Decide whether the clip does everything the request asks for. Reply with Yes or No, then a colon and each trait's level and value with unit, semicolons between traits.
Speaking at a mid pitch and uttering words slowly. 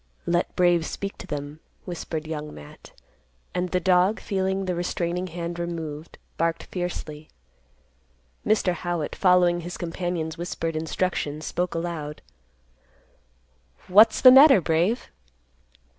Yes: medium, 175 Hz; slow, 115 wpm